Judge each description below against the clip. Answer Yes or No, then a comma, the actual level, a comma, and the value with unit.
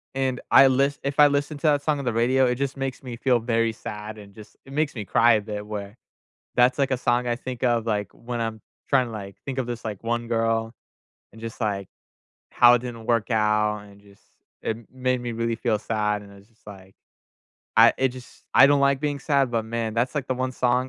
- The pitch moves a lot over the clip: No, average, 3.1 semitones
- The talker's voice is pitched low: Yes, low, 120 Hz